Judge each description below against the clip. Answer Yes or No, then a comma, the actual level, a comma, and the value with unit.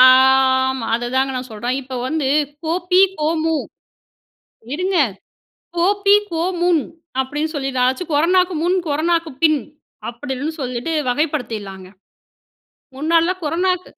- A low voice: No, very high, 300 Hz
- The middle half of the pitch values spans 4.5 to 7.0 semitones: Yes, average, 4.8 semitones